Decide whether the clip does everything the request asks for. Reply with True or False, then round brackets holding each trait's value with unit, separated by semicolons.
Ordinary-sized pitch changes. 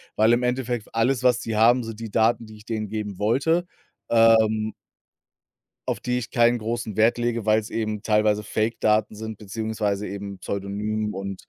False (1.7 semitones)